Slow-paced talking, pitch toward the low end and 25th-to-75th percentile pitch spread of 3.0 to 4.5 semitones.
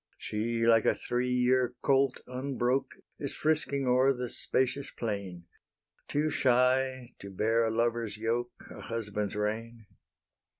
No: slow, 130 wpm; low, 120 Hz; narrow, 2.5 semitones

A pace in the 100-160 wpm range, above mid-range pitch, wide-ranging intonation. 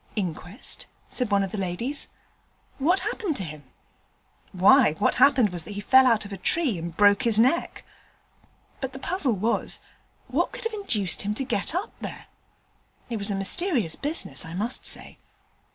No: average, 180 wpm; high, 220 Hz; wide, 5.9 semitones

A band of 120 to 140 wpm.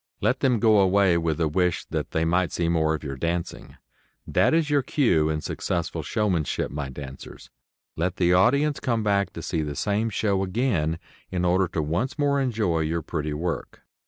No: average, 190 wpm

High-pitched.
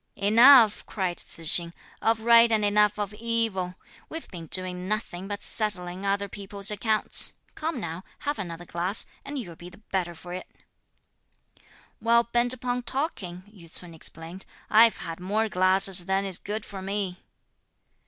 Yes: high, 200 Hz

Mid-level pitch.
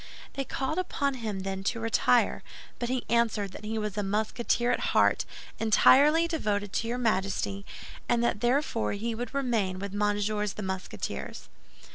No: high, 220 Hz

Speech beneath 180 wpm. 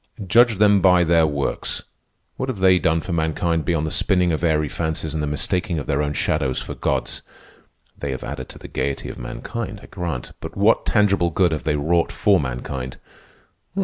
No: average, 195 wpm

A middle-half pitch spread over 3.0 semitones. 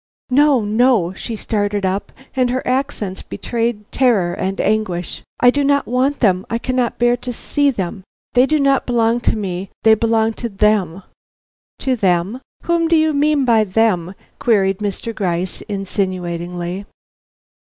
Yes: average, 4.7 semitones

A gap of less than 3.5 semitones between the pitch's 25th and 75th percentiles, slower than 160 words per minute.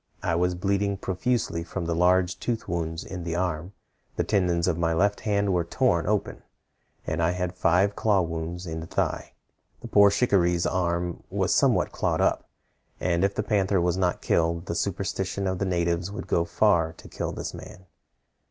No: narrow, 2.6 semitones; average, 180 wpm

